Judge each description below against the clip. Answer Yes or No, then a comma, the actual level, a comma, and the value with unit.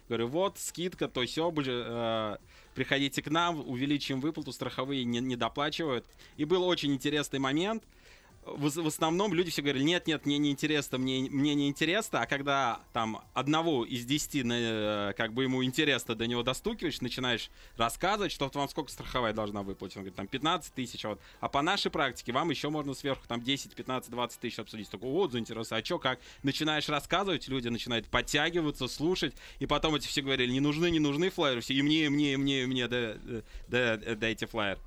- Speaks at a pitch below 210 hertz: Yes, low, 135 Hz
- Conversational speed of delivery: No, fast, 205 wpm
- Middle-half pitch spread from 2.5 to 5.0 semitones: Yes, average, 4.2 semitones